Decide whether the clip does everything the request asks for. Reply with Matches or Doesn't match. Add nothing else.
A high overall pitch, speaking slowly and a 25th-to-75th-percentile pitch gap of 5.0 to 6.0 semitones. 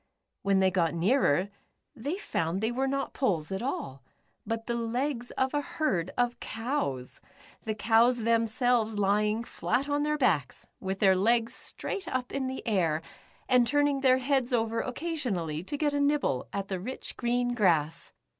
Doesn't match